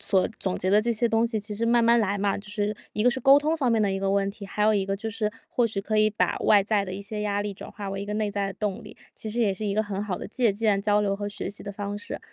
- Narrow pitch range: Yes, narrow, 1.8 semitones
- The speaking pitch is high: Yes, high, 210 Hz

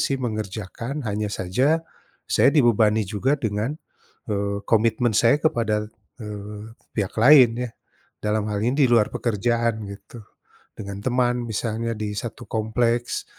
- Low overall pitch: Yes, low, 115 Hz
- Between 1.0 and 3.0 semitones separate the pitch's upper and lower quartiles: Yes, narrow, 2.6 semitones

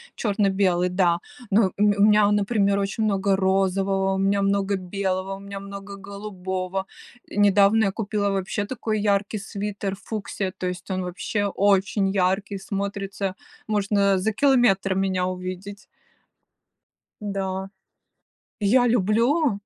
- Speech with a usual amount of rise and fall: No, narrow, 1.2 semitones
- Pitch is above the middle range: Yes, high, 200 Hz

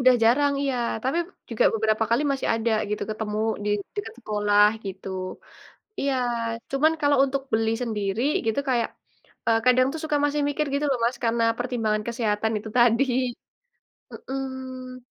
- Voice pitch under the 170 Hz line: No, high, 240 Hz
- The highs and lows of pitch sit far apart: No, average, 3.5 semitones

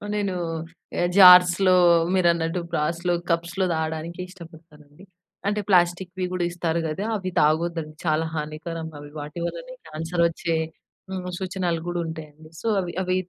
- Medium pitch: Yes, medium, 170 Hz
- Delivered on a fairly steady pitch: Yes, narrow, 2.2 semitones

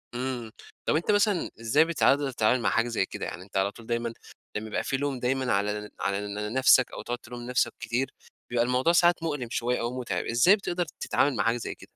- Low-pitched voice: Yes, low, 120 Hz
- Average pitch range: Yes, average, 3.1 semitones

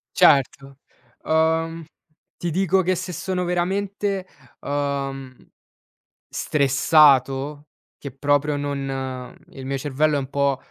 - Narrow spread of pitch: No, average, 3.6 semitones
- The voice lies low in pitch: No, medium, 145 Hz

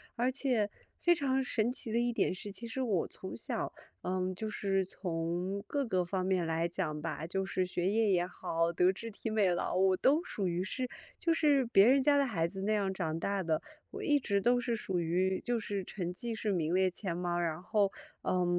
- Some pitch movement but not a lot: Yes, average, 4.6 semitones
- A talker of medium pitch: No, high, 195 Hz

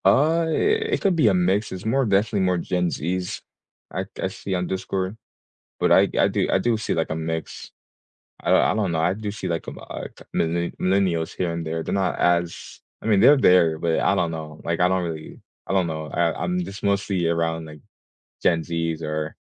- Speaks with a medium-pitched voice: No, very low, 90 Hz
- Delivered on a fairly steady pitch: No, average, 3.4 semitones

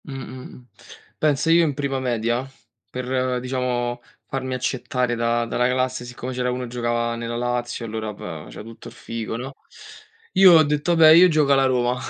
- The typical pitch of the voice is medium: No, low, 125 Hz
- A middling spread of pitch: No, narrow, 2.1 semitones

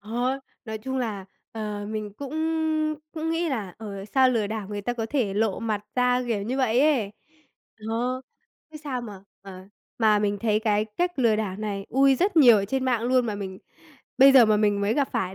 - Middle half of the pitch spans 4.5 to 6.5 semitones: No, average, 3.8 semitones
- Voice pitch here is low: No, high, 220 Hz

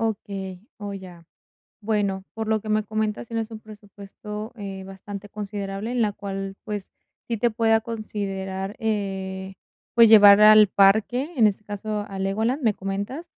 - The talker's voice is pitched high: Yes, high, 210 Hz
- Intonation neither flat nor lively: No, narrow, 2.1 semitones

